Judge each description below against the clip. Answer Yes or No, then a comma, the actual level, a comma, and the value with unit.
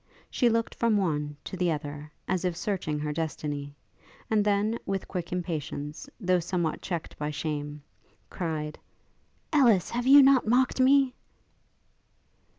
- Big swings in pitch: Yes, wide, 6.4 semitones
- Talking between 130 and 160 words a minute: Yes, average, 140 wpm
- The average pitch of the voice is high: No, medium, 180 Hz